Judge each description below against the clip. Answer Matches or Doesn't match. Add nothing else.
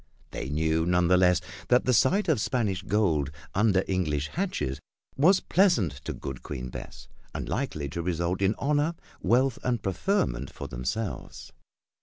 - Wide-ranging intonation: Matches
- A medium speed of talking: Matches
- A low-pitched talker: Matches